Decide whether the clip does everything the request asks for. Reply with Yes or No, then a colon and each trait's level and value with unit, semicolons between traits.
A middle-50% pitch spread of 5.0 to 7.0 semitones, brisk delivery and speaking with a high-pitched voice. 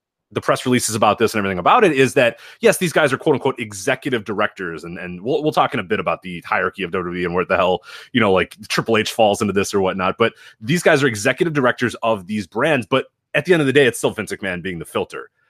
No: wide, 5.5 semitones; fast, 265 wpm; low, 125 Hz